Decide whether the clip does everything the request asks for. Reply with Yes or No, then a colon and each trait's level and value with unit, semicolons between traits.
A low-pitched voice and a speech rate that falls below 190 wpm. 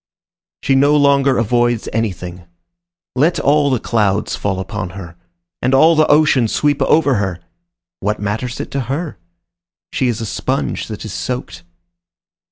Yes: low, 120 Hz; average, 150 wpm